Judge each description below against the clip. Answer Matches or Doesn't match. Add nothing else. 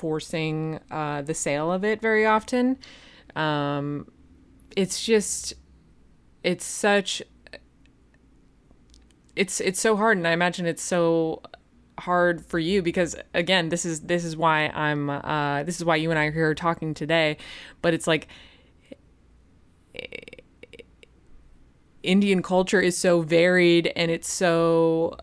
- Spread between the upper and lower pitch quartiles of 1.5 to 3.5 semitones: Matches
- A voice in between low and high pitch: Matches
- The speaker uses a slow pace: Matches